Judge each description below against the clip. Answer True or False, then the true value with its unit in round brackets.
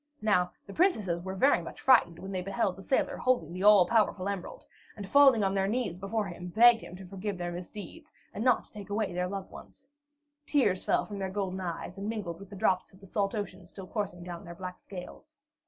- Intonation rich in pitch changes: False (2.9 semitones)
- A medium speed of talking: False (225 wpm)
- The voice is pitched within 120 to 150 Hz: False (195 Hz)